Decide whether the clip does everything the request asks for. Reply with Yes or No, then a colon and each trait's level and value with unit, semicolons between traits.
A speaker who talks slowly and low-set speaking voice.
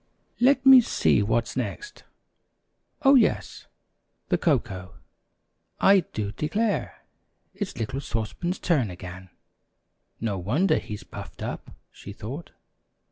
Yes: slow, 115 wpm; low, 130 Hz